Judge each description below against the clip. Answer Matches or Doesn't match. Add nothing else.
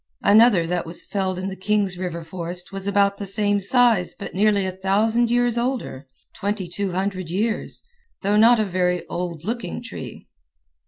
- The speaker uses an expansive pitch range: Doesn't match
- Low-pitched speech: Doesn't match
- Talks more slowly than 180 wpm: Matches